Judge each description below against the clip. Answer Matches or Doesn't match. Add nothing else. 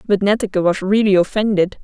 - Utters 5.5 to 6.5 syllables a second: Matches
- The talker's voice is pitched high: Matches